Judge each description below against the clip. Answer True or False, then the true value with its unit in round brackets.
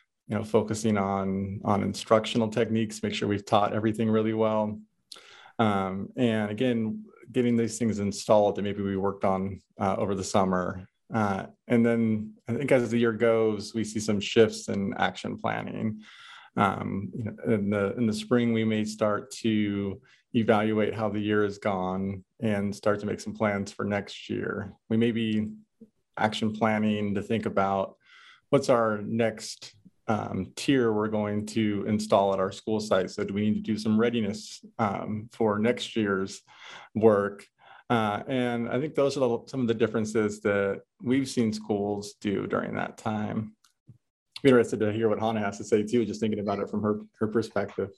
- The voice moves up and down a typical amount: False (1.9 semitones)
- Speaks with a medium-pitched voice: False (110 Hz)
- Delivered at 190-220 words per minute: False (180 wpm)